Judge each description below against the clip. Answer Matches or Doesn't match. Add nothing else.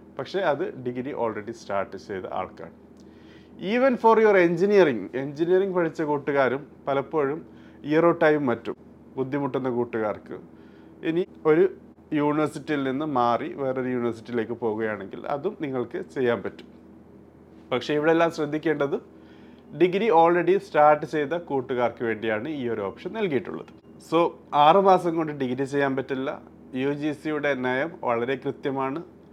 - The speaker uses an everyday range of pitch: Matches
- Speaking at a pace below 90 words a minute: Doesn't match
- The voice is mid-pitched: Matches